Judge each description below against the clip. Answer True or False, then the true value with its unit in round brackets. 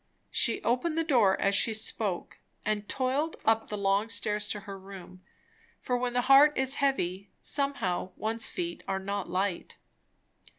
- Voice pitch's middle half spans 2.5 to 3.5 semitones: False (4.7 semitones)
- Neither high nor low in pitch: False (215 Hz)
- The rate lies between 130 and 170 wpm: True (160 wpm)